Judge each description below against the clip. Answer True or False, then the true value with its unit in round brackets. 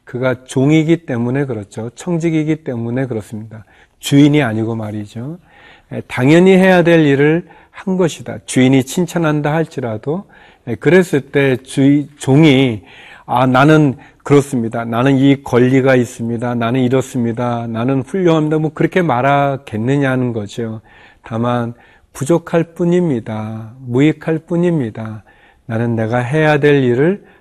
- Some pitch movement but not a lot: True (4.8 semitones)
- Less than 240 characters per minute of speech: False (290 characters per minute)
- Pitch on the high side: False (135 Hz)